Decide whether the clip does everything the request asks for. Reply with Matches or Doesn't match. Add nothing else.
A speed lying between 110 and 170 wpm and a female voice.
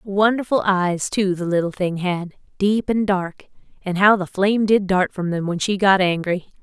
Doesn't match